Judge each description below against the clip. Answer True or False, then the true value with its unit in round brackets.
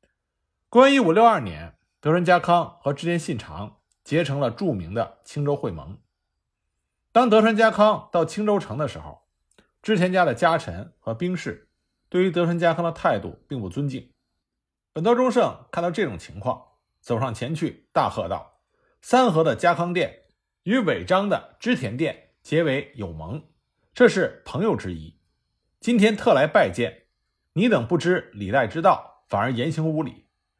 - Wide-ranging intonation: True (8.5 semitones)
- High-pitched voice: False (160 Hz)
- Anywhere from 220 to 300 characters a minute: True (235 characters per minute)